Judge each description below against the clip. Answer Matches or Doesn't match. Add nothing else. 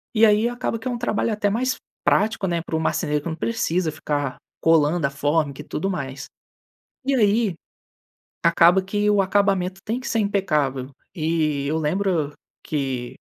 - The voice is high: Doesn't match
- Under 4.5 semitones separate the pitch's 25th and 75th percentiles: Doesn't match